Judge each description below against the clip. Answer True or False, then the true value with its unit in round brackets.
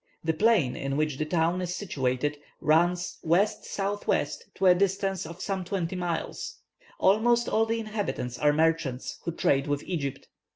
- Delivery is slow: False (155 wpm)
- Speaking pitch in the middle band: True (175 Hz)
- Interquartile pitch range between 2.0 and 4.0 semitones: False (4.7 semitones)